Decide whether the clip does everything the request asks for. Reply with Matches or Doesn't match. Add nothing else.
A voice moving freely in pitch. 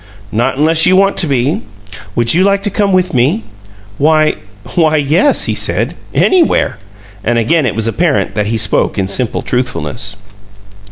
Matches